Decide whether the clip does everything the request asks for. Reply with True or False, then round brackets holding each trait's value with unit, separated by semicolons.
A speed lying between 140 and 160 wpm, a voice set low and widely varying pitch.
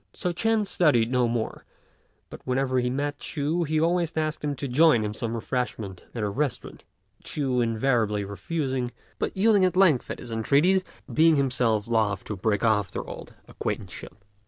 False (170 wpm; 130 Hz; 5.8 semitones)